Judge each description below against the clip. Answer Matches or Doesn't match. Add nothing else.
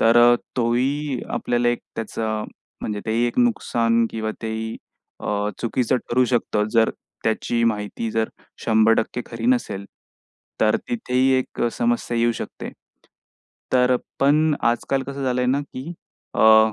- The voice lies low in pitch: Matches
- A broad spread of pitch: Doesn't match